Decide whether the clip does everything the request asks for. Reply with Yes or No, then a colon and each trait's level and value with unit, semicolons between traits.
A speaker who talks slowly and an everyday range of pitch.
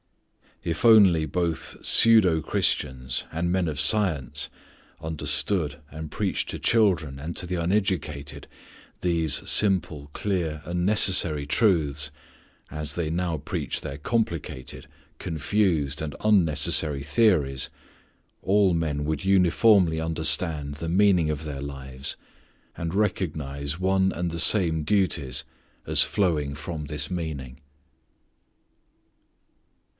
Yes: slow, 110 wpm; average, 4.0 semitones